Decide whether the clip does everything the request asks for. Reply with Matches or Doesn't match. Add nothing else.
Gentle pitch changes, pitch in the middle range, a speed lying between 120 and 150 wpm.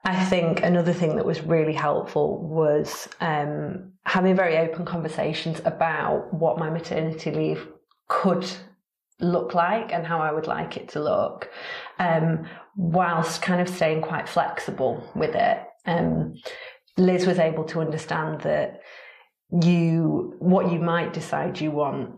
Matches